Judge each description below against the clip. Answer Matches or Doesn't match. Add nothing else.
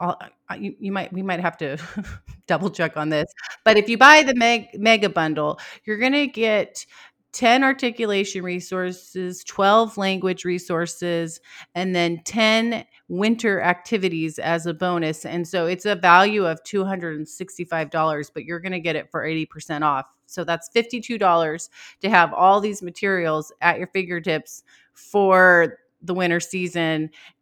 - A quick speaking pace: Doesn't match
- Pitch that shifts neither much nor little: Matches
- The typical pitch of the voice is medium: Matches